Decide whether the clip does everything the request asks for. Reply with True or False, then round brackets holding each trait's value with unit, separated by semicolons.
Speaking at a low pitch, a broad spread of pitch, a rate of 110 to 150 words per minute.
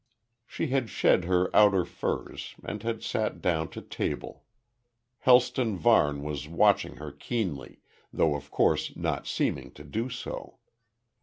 True (90 Hz; 7.3 semitones; 140 wpm)